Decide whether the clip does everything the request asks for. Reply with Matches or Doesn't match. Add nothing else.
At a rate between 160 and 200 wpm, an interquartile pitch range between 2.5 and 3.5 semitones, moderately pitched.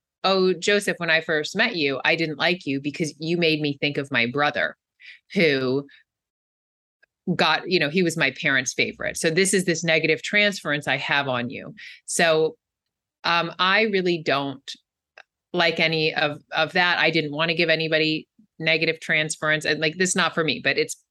Matches